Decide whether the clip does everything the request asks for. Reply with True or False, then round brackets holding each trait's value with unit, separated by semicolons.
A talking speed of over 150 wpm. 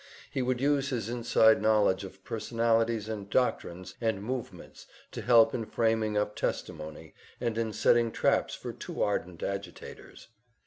False (145 wpm)